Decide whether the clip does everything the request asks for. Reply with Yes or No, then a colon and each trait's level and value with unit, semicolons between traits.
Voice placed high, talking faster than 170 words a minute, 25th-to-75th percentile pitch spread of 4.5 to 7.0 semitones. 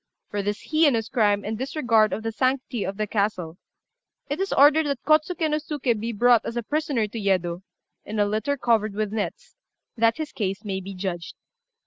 Yes: high, 225 Hz; average, 190 wpm; average, 5.2 semitones